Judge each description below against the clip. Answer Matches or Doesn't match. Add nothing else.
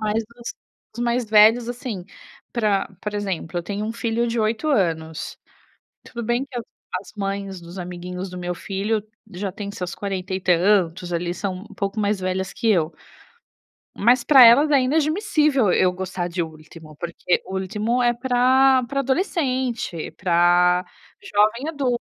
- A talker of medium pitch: Doesn't match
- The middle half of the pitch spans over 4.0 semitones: Matches